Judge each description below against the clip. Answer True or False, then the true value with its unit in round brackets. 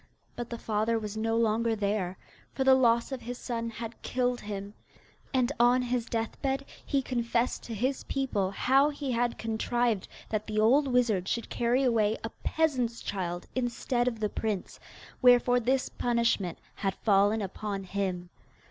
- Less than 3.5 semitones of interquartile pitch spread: True (2.8 semitones)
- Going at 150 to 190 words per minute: True (160 wpm)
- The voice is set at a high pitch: True (230 Hz)